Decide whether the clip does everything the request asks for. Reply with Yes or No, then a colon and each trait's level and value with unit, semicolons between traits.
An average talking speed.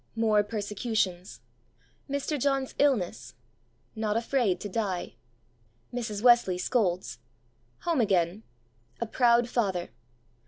No: slow, 95 wpm